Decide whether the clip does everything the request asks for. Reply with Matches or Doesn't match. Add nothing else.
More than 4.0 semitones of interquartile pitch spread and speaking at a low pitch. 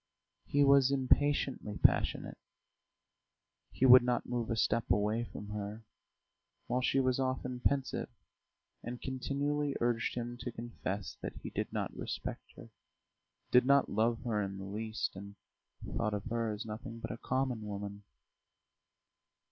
Doesn't match